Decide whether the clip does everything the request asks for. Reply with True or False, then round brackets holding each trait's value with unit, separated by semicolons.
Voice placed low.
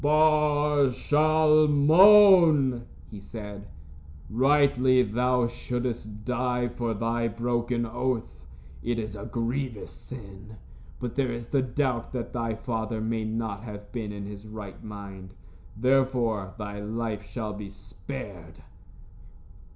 True (120 Hz)